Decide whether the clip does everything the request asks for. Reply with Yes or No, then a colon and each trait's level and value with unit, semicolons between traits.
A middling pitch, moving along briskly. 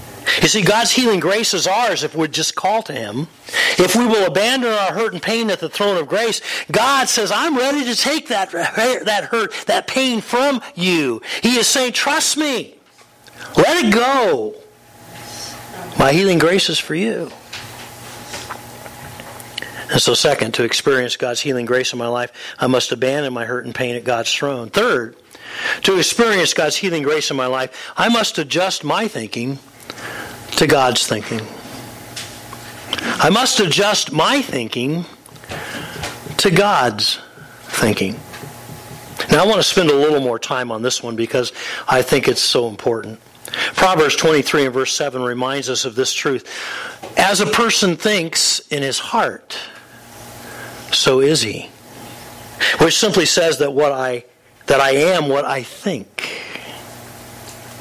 No: medium, 170 Hz; average, 155 wpm